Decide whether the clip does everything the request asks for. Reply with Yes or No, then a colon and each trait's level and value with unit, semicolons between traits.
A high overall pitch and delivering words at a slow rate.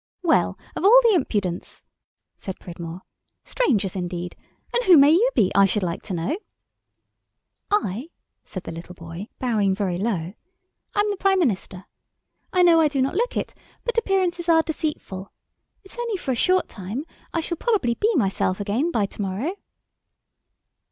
No: very high, 250 Hz; average, 165 wpm